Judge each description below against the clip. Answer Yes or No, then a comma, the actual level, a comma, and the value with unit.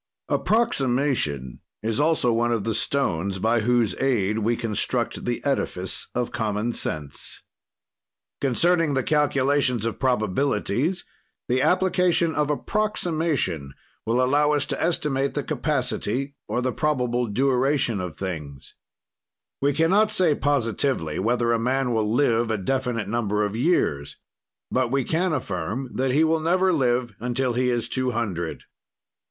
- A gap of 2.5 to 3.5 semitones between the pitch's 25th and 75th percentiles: No, average, 4.5 semitones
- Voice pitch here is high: No, low, 125 Hz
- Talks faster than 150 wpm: No, average, 140 wpm